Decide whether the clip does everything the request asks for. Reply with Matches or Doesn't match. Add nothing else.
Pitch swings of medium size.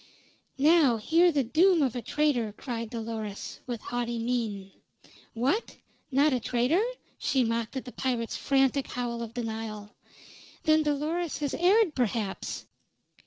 Matches